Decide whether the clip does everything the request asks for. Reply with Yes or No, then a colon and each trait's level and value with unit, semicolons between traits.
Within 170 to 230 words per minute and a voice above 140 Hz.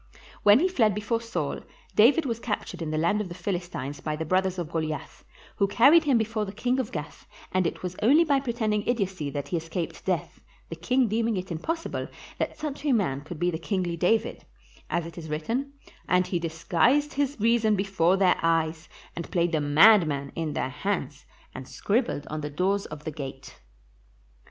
Yes: average, 195 wpm; medium, 185 Hz